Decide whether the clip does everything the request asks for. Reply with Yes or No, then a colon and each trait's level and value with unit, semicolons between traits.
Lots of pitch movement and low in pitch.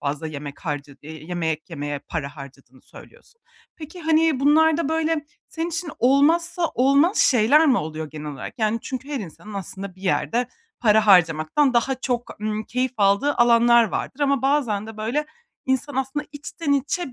No: wide, 8.7 semitones; high, 240 Hz